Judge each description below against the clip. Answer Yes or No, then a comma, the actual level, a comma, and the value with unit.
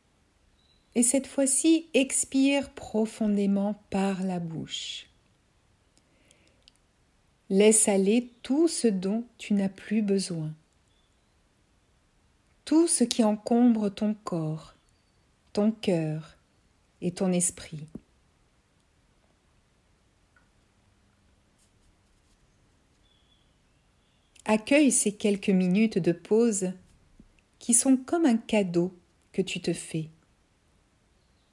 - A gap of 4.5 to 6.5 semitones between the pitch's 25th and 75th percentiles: Yes, average, 4.8 semitones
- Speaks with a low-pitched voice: No, high, 210 Hz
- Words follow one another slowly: Yes, slow, 80 wpm